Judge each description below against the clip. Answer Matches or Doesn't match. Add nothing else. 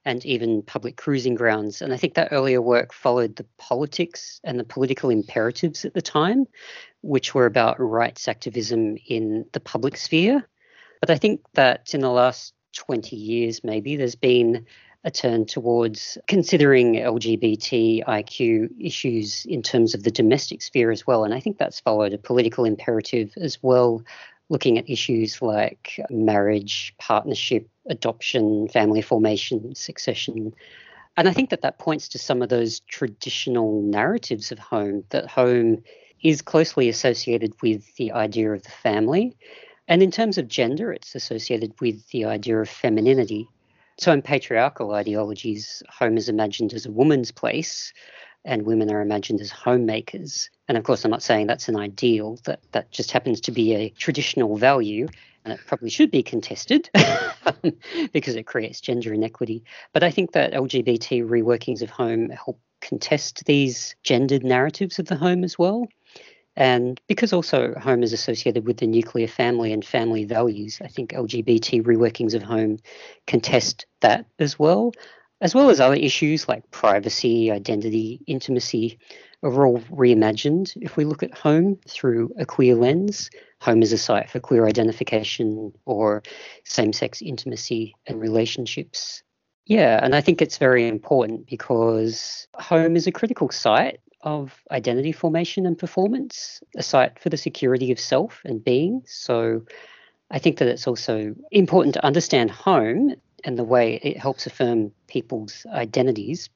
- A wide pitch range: Matches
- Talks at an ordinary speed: Matches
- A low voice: Matches